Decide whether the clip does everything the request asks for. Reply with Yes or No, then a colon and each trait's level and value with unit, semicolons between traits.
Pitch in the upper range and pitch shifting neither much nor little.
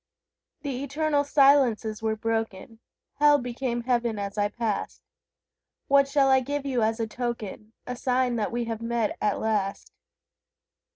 Yes: high, 235 Hz; average, 3.5 semitones